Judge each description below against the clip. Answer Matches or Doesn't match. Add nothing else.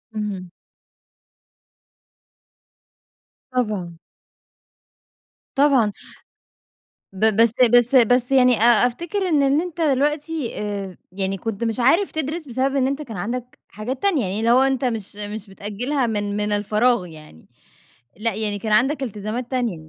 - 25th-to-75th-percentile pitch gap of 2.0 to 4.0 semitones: Doesn't match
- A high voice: Matches